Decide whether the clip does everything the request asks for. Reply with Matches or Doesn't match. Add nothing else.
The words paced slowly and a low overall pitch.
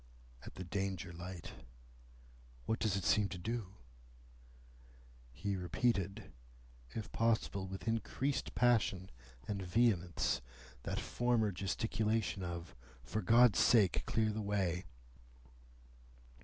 Matches